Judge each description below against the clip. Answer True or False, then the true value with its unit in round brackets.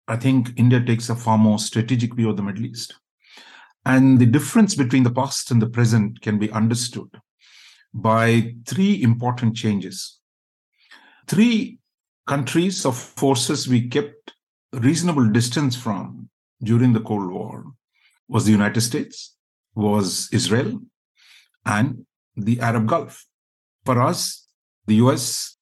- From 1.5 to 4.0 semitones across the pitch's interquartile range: True (3.2 semitones)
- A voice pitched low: True (120 Hz)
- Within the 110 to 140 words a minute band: True (135 wpm)